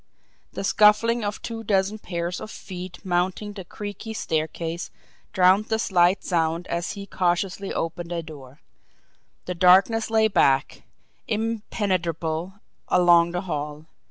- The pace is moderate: No, slow, 130 wpm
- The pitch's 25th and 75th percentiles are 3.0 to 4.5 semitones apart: Yes, average, 3.4 semitones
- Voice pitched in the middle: Yes, medium, 180 Hz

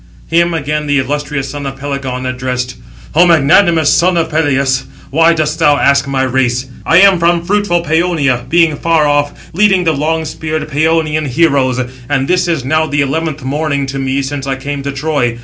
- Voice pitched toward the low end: No, medium, 145 Hz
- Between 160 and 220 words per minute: Yes, average, 185 wpm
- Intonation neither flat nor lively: Yes, average, 3.1 semitones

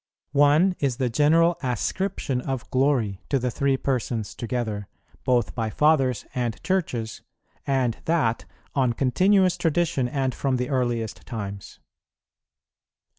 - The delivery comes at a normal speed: No, slow, 125 wpm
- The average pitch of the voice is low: Yes, low, 130 Hz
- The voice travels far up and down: No, average, 3.8 semitones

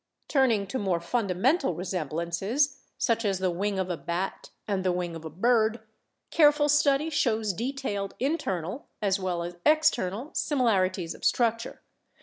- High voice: Yes, high, 205 Hz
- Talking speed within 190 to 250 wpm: No, average, 150 wpm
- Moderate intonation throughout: No, wide, 6.5 semitones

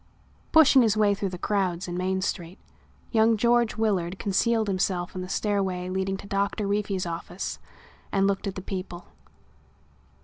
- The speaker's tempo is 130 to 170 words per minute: Yes, average, 160 wpm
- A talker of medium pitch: No, high, 195 Hz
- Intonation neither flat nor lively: No, narrow, 2.3 semitones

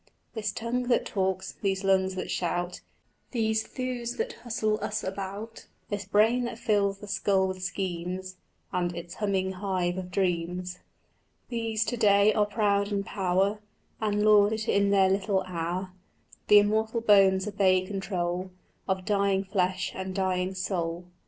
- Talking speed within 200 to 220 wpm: No, average, 150 wpm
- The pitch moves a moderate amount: No, narrow, 2.2 semitones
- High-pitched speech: Yes, high, 195 Hz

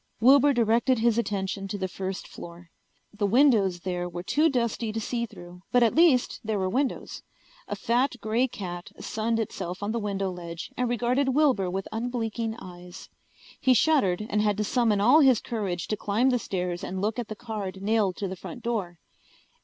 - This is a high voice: Yes, high, 215 Hz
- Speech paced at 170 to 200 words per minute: Yes, average, 190 wpm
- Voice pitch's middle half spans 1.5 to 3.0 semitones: No, average, 4.2 semitones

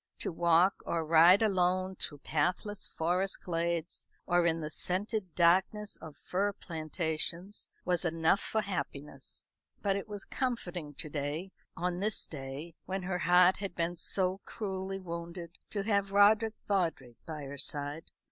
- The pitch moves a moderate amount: Yes, average, 3.1 semitones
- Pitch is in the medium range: Yes, medium, 180 Hz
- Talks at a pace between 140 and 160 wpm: Yes, average, 145 wpm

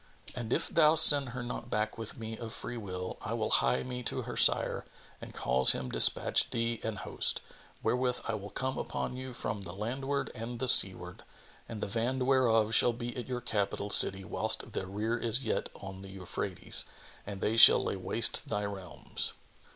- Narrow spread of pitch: No, average, 3.6 semitones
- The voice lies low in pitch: Yes, low, 115 Hz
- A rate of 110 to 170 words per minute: No, average, 190 wpm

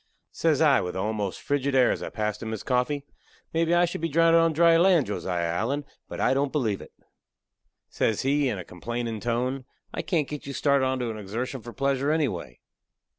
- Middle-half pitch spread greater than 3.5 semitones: Yes, average, 5.1 semitones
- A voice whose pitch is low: Yes, low, 130 Hz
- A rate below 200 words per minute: No, fast, 205 wpm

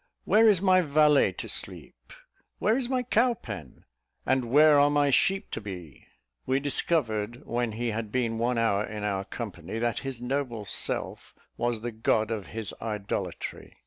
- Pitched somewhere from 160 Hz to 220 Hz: No, low, 120 Hz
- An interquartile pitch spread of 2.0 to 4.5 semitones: No, average, 5.2 semitones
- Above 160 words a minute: Yes, average, 170 wpm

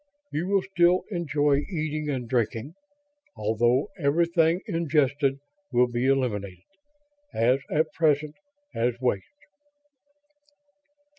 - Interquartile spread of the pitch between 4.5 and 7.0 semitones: Yes, average, 5.0 semitones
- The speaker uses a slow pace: Yes, slow, 95 wpm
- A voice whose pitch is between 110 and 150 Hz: Yes, medium, 140 Hz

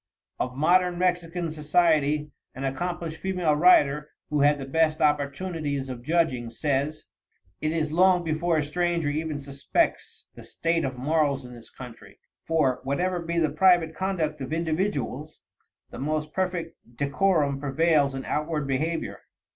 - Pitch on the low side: No, medium, 155 Hz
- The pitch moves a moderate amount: Yes, average, 3.3 semitones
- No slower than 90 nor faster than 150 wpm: Yes, average, 145 wpm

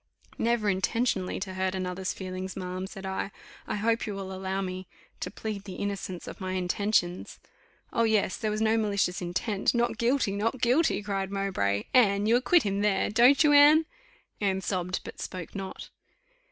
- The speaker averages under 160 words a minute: No, average, 175 wpm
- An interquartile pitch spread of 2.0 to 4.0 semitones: Yes, average, 3.0 semitones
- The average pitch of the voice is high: Yes, high, 200 Hz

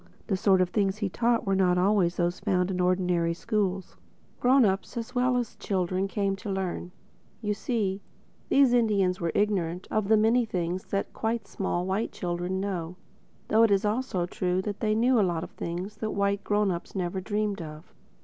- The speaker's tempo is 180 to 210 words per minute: Yes, average, 190 wpm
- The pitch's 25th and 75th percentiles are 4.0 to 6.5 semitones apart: No, average, 2.9 semitones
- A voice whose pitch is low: No, high, 195 Hz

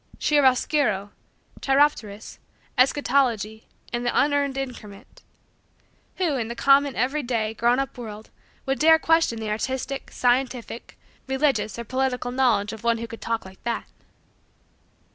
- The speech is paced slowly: Yes, slow, 130 wpm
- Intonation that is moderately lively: Yes, average, 3.4 semitones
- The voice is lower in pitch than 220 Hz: No, very high, 250 Hz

